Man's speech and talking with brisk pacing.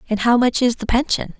No: female; fast, 260 wpm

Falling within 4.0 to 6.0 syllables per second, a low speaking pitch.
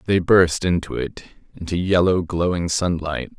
Yes: 4.5 syllables/s; very low, 85 Hz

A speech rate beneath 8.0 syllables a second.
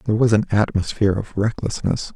Yes: 6.3 syllables/s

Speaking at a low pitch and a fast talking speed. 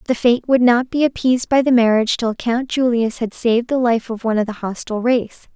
No: high, 240 Hz; fast, 240 wpm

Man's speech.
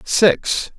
Yes: male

